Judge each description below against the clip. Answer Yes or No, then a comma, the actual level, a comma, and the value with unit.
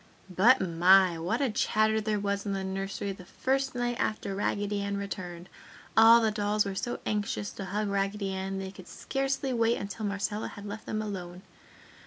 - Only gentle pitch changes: Yes, narrow, 2.1 semitones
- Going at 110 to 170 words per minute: No, average, 185 wpm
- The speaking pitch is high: Yes, high, 205 Hz